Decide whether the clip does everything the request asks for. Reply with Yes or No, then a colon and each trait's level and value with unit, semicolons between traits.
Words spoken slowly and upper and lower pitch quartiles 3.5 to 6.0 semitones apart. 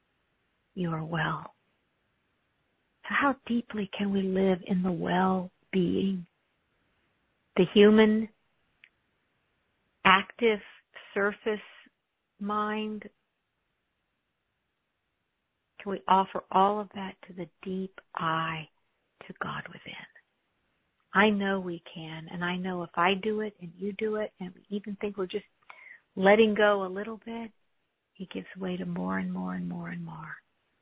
Yes: slow, 130 wpm; average, 4.3 semitones